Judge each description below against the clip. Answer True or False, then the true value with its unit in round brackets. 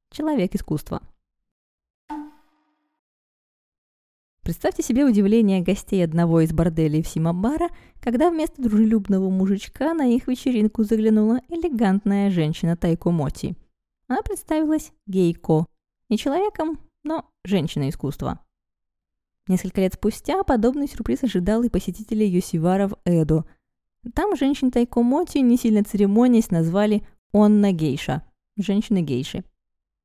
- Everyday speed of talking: False (105 wpm)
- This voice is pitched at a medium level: False (210 Hz)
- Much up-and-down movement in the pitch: True (7.2 semitones)